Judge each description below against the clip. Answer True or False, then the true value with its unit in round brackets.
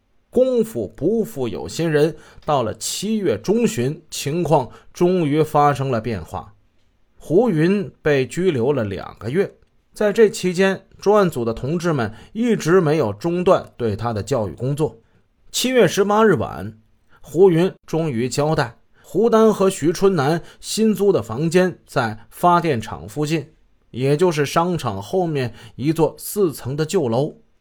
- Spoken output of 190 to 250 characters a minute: True (215 characters per minute)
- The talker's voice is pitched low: False (155 Hz)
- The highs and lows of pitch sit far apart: True (8.0 semitones)